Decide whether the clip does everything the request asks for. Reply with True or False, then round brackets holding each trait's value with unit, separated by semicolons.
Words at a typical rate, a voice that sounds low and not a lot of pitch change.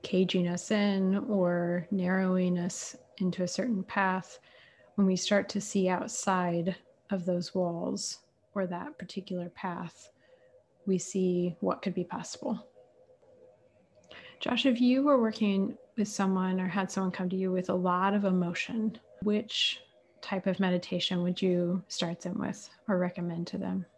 False (150 wpm; 190 Hz; 2.1 semitones)